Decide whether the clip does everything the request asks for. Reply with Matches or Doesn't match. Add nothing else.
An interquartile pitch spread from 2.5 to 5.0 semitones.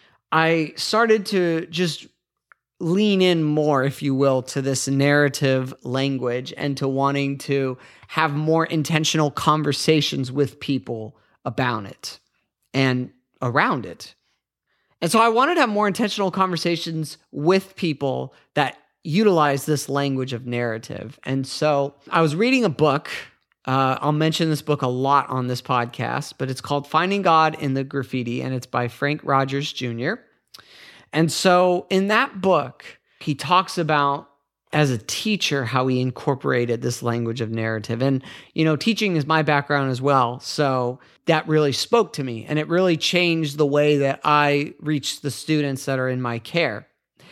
Matches